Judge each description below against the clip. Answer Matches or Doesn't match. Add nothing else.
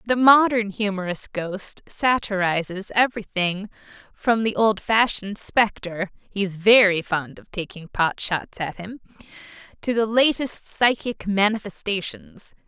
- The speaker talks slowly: Matches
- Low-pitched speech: Doesn't match